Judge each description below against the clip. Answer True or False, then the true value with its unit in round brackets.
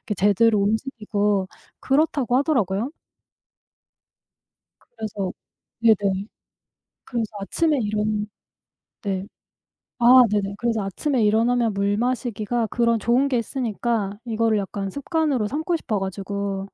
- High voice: True (220 Hz)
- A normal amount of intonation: True (3.4 semitones)